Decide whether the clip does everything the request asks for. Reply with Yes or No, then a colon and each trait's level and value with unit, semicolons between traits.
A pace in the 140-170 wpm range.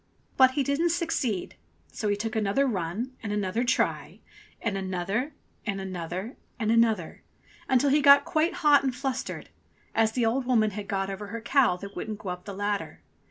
No: average, 180 wpm